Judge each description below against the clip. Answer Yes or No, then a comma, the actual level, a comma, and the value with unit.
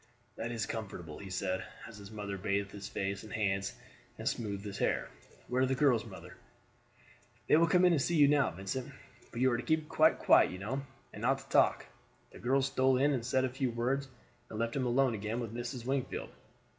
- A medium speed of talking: No, fast, 220 wpm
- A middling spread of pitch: Yes, average, 4.7 semitones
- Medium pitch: No, low, 120 Hz